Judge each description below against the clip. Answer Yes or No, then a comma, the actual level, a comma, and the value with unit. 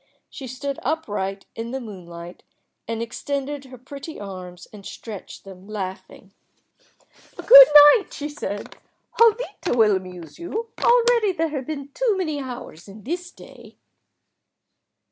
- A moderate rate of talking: No, slow, 130 wpm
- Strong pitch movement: Yes, wide, 8.4 semitones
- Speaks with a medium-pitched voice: No, very high, 260 Hz